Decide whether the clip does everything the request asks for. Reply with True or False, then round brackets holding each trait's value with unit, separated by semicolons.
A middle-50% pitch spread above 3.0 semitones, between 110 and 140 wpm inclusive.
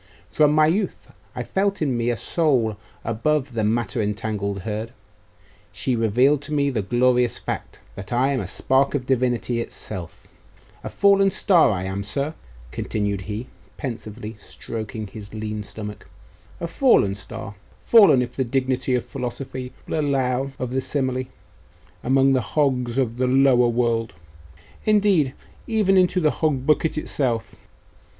False (4.3 semitones; 150 wpm)